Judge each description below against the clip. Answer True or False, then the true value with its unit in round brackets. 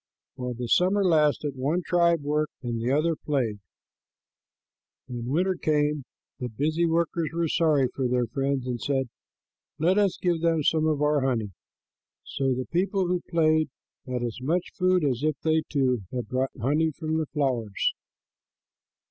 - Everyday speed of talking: True (160 wpm)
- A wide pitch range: False (4.3 semitones)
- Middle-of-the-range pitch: True (150 Hz)